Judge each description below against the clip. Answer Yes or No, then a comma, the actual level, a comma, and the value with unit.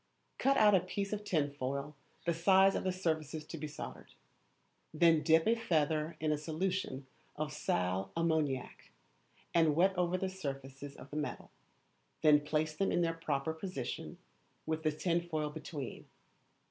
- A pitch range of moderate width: Yes, average, 3.1 semitones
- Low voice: No, medium, 160 Hz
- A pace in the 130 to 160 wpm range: Yes, average, 155 wpm